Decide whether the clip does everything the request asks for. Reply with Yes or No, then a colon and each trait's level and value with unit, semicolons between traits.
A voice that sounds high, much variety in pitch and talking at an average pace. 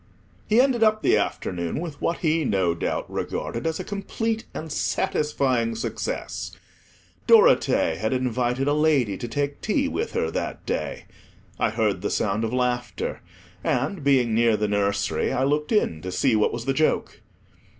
No: low, 130 Hz; wide, 6.5 semitones; average, 165 wpm